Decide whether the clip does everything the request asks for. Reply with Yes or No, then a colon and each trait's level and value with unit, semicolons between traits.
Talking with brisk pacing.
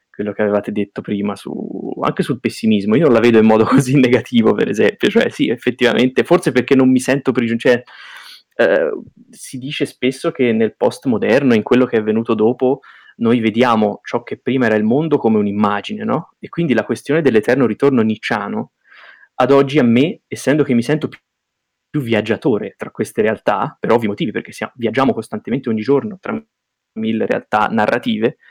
Yes: fast, 180 wpm